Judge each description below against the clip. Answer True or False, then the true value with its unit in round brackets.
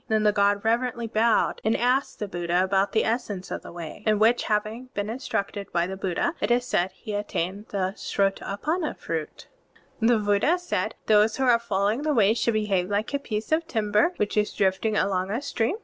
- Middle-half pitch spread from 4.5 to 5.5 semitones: False (3.0 semitones)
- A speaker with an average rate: False (210 wpm)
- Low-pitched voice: False (210 Hz)